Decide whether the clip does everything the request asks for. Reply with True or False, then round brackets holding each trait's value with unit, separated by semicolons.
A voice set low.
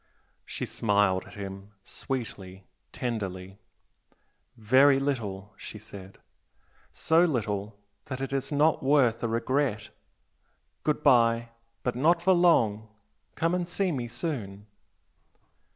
True (115 Hz)